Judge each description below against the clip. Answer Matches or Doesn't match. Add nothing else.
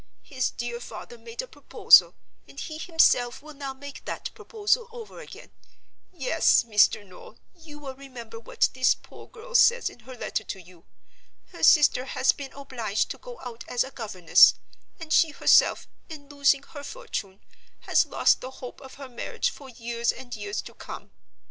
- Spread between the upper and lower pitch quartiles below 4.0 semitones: Doesn't match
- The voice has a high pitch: Matches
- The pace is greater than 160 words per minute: Matches